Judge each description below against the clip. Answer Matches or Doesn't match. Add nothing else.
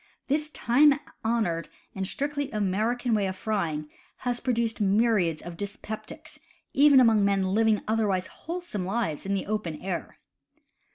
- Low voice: Doesn't match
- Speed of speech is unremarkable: Matches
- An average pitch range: Matches